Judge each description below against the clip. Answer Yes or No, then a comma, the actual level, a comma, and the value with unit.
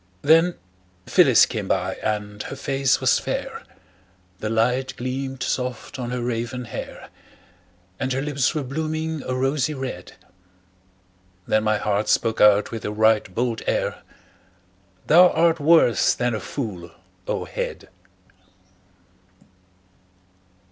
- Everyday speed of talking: No, slow, 125 wpm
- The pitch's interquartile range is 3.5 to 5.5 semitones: Yes, average, 4.2 semitones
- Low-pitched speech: Yes, low, 125 Hz